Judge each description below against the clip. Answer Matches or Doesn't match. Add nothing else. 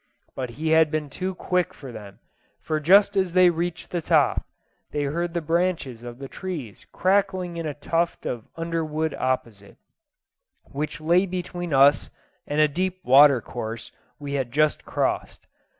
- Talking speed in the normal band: Matches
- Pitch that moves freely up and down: Doesn't match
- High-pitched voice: Doesn't match